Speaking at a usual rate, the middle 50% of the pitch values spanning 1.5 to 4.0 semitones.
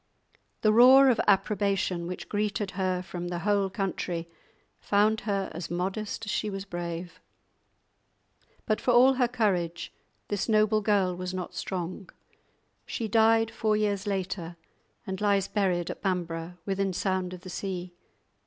Yes: average, 145 wpm; average, 2.9 semitones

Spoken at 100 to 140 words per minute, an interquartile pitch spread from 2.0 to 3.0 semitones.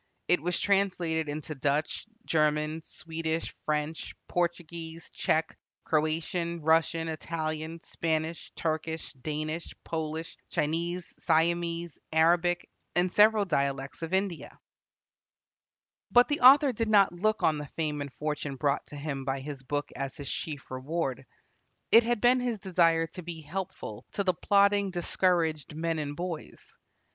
Yes: slow, 135 wpm; narrow, 2.6 semitones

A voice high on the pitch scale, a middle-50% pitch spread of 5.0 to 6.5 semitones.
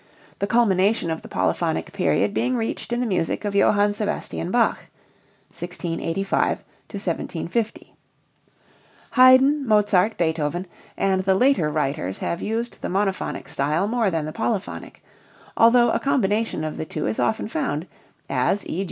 Yes: high, 195 Hz; wide, 5.4 semitones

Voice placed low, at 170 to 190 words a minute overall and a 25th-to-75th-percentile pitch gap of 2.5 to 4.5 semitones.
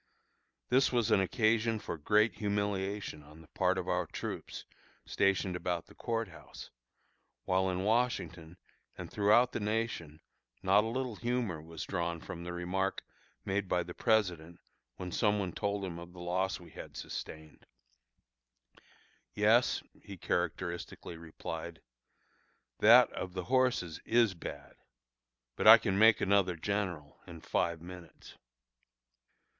No: very low, 95 Hz; average, 140 wpm; average, 3.5 semitones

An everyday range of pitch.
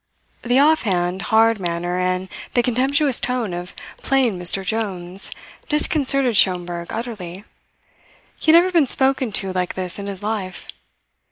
No: wide, 5.8 semitones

